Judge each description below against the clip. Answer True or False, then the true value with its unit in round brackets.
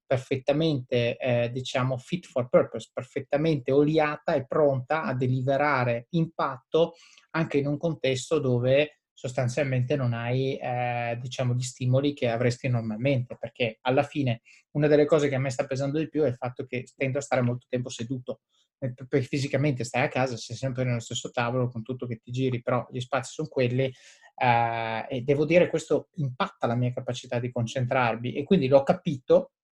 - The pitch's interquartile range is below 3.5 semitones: True (2.8 semitones)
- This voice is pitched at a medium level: False (130 Hz)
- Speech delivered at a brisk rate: True (175 wpm)